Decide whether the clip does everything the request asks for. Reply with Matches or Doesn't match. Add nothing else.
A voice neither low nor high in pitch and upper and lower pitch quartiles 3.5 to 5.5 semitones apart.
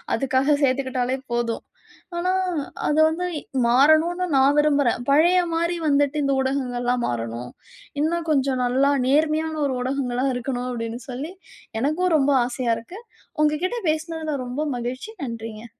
Doesn't match